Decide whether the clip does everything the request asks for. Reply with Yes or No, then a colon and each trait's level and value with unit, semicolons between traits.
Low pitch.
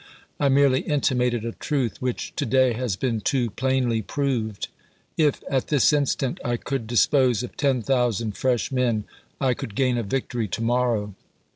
Yes: low, 125 Hz